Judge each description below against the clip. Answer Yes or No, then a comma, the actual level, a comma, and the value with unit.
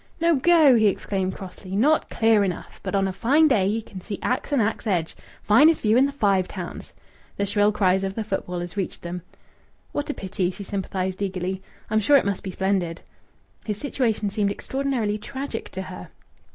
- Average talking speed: Yes, average, 190 wpm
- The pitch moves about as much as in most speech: Yes, average, 3.8 semitones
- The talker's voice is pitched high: Yes, high, 205 Hz